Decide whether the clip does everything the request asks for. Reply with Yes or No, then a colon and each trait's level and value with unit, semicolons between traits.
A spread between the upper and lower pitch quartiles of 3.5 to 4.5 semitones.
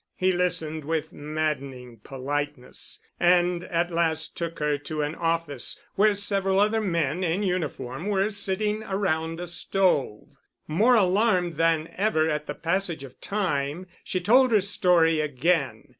Yes: average, 4.0 semitones